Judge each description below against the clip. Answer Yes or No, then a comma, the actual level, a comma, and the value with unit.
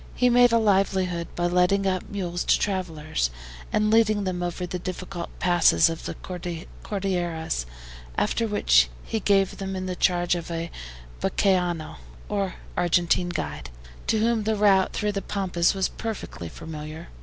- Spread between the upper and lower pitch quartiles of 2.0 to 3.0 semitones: Yes, narrow, 2.6 semitones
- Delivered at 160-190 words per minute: No, average, 150 wpm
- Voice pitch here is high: No, medium, 180 Hz